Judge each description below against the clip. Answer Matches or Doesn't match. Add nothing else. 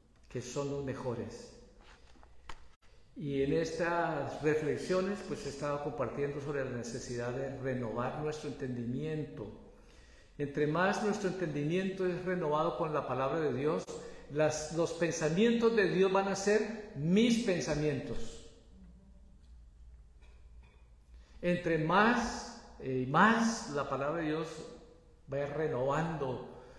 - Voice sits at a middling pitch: Matches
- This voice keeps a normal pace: Doesn't match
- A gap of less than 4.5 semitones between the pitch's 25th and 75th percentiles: Doesn't match